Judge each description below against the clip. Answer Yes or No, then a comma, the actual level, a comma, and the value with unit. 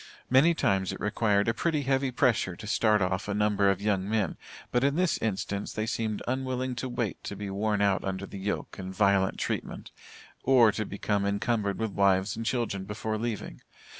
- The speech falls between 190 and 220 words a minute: Yes, average, 195 wpm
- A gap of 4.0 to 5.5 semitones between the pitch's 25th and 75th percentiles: No, average, 3.2 semitones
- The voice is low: Yes, low, 105 Hz